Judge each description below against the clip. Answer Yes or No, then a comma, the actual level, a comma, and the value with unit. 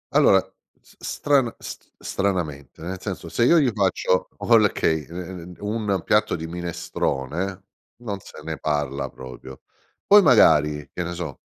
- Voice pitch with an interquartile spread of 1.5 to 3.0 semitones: No, average, 5.0 semitones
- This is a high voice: No, very low, 90 Hz